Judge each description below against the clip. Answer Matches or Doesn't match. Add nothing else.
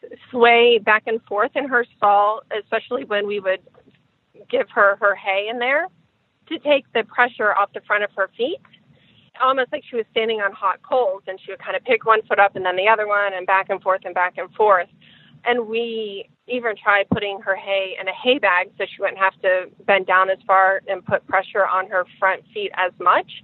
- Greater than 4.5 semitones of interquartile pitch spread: Doesn't match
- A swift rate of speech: Matches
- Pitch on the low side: Doesn't match